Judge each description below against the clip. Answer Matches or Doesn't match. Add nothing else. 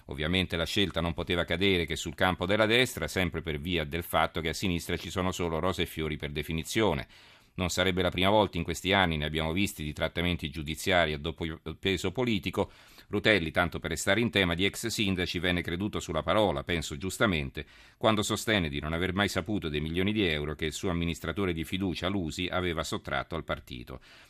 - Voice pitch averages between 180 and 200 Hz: Doesn't match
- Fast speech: Matches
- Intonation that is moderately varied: Matches